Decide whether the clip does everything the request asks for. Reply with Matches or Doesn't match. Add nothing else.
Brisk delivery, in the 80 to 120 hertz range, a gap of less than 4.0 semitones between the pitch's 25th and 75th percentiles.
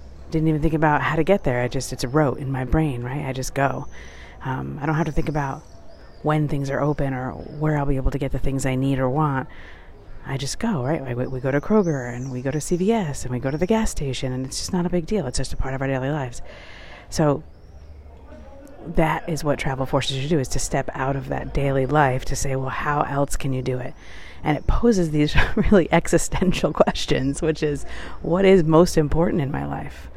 Doesn't match